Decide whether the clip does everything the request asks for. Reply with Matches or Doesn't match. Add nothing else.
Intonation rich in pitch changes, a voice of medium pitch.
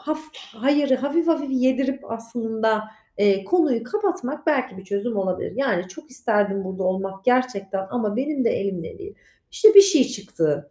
Doesn't match